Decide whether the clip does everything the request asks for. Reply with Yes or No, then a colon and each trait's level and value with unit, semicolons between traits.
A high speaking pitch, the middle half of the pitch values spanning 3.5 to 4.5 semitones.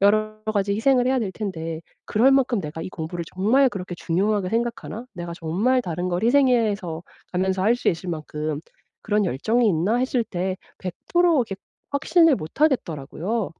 No: high, 200 Hz; wide, 5.6 semitones